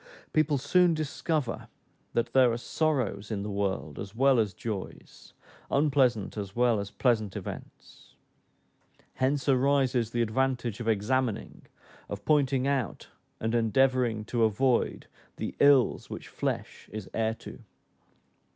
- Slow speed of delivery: Yes, slow, 130 wpm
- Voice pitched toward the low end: Yes, low, 120 Hz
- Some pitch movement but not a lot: Yes, average, 3.7 semitones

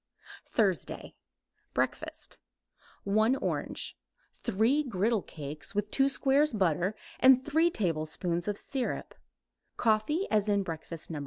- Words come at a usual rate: No, slow, 105 wpm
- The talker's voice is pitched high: Yes, high, 215 Hz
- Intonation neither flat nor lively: No, wide, 6.8 semitones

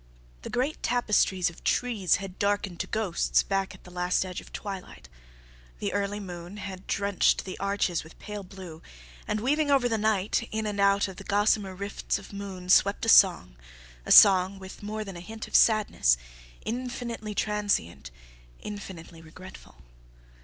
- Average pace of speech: Yes, average, 165 wpm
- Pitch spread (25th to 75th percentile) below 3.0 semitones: Yes, narrow, 2.6 semitones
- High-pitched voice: Yes, high, 200 Hz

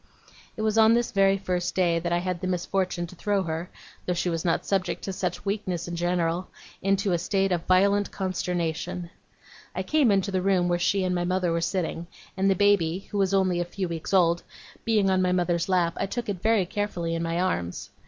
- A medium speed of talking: No, fast, 220 wpm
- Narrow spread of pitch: Yes, narrow, 2.2 semitones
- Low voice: No, medium, 185 Hz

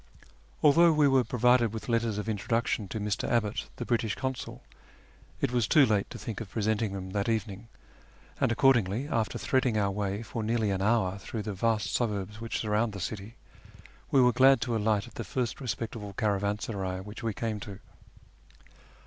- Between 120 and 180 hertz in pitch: No, low, 110 Hz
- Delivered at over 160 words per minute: Yes, average, 180 wpm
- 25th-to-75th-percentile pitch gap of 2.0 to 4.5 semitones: Yes, average, 2.7 semitones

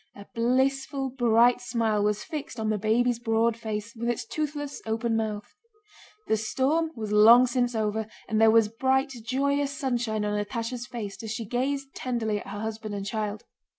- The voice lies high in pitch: Yes, high, 230 Hz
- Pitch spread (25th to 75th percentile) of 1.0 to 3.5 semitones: Yes, average, 2.9 semitones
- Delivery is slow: No, average, 175 wpm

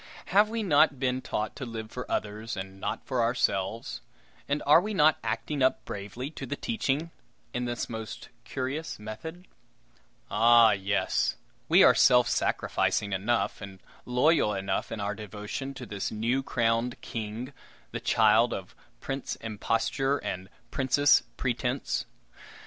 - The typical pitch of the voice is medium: No, low, 120 Hz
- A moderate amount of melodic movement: Yes, average, 4.1 semitones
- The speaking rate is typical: Yes, average, 145 wpm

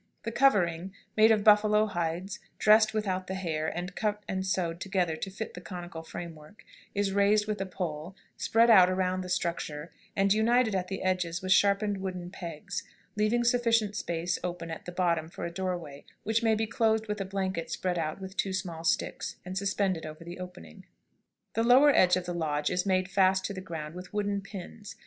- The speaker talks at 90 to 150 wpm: No, average, 195 wpm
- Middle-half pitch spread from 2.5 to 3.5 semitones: Yes, average, 3.1 semitones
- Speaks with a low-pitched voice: No, high, 190 Hz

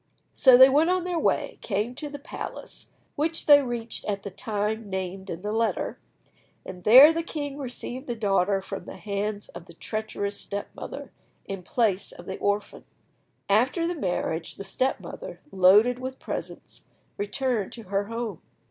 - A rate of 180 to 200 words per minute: No, average, 170 wpm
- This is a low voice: No, high, 215 Hz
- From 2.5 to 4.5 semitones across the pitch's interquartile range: No, average, 4.9 semitones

